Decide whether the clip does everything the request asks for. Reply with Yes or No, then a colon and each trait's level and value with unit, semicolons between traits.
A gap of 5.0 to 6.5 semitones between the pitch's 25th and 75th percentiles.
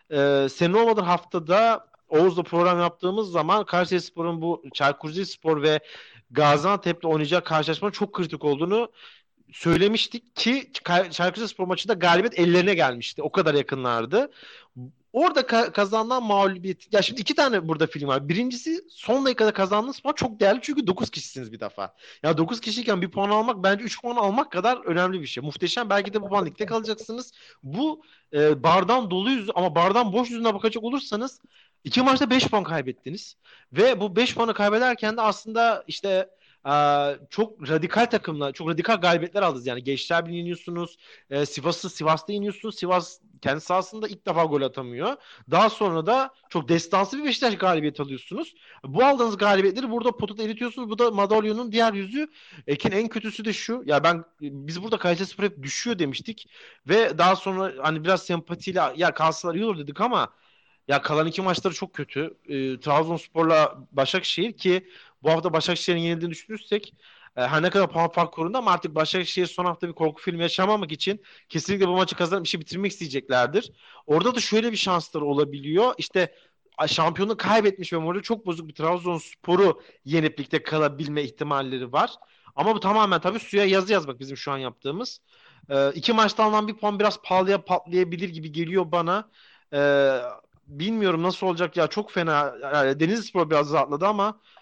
Yes: average, 5.3 semitones